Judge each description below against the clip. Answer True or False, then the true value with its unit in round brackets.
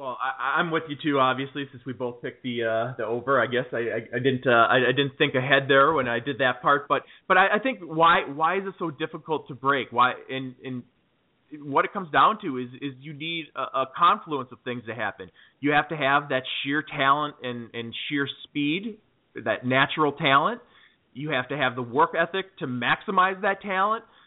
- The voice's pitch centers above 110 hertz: True (140 Hz)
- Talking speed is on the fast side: True (225 wpm)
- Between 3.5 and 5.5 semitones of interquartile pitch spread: True (4.0 semitones)